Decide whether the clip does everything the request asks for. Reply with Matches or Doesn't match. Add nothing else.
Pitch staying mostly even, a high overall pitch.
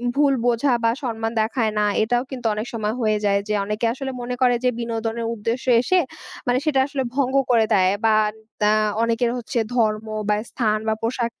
Matches